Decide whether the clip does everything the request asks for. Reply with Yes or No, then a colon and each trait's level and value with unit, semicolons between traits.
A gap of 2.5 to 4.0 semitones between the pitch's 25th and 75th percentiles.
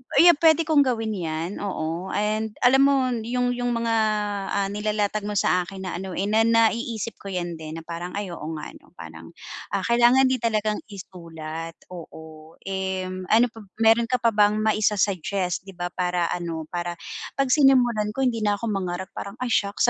No: average, 4.5 semitones